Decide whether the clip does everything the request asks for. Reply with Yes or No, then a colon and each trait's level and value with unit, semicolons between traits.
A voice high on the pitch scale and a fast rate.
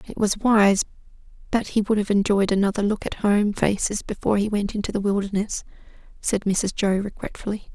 No: high, 205 Hz; average, 180 wpm